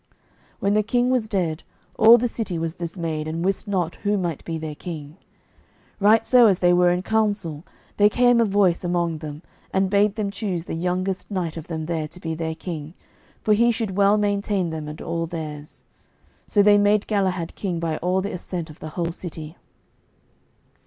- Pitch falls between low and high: Yes, medium, 180 Hz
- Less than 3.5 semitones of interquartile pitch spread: No, average, 3.8 semitones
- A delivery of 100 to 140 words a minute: No, average, 195 wpm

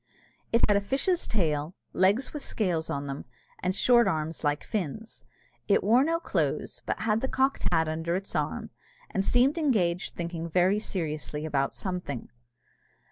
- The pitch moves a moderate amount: No, wide, 6.1 semitones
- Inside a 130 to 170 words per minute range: Yes, average, 160 wpm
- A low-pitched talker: No, medium, 185 Hz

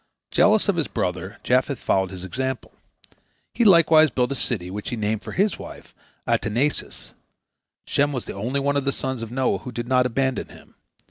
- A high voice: No, low, 130 Hz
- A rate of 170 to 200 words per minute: Yes, average, 190 wpm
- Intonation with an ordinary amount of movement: Yes, average, 4.3 semitones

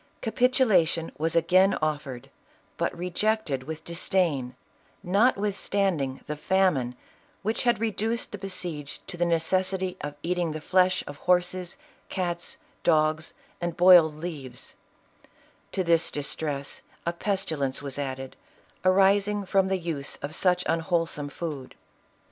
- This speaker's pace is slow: Yes, slow, 125 wpm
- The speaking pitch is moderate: Yes, medium, 175 Hz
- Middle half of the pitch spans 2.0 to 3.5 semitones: No, average, 4.0 semitones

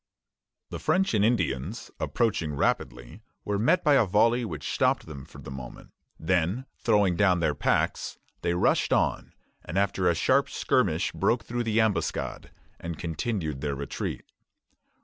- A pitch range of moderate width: No, wide, 6.6 semitones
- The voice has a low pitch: Yes, very low, 95 Hz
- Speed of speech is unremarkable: Yes, average, 150 wpm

